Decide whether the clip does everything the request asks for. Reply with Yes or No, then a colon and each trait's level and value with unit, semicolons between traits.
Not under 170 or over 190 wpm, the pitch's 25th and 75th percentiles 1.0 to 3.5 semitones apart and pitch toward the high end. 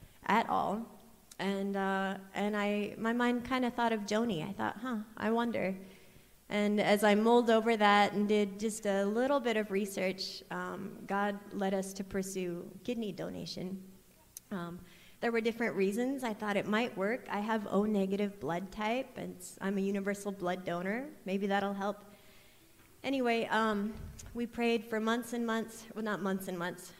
Yes: average, 175 wpm; narrow, 2.6 semitones; high, 205 Hz